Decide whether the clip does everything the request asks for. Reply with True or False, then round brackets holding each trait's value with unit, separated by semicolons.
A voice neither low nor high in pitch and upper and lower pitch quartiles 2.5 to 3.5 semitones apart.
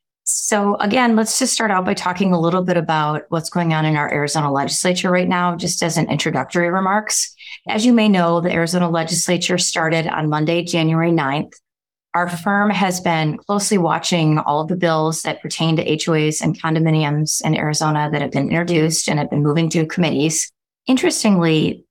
True (170 Hz; 2.9 semitones)